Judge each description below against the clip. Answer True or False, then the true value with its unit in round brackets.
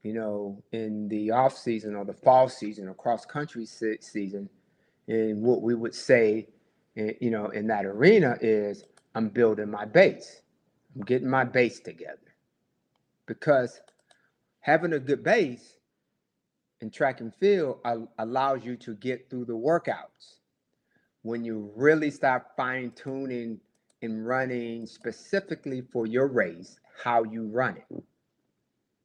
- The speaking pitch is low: True (115 Hz)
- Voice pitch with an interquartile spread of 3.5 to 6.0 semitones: False (2.8 semitones)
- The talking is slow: True (130 wpm)